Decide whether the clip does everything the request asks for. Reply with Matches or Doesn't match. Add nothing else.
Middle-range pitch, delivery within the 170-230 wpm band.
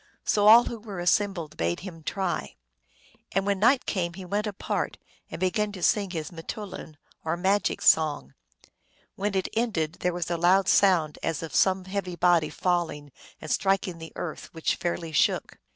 Matches